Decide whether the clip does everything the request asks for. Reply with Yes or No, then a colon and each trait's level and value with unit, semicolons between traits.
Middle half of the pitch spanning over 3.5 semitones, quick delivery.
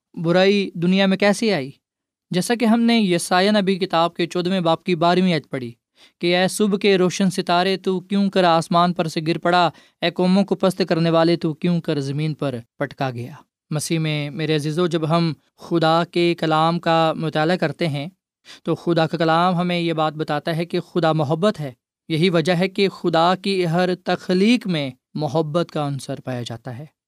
No: average, 2.9 semitones; fast, 195 wpm